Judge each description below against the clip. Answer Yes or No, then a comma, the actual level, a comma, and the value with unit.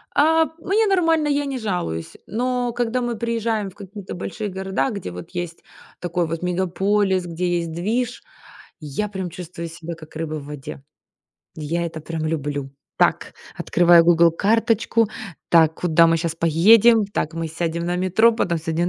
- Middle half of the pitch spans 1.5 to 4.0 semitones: No, average, 5.2 semitones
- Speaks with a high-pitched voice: No, medium, 180 Hz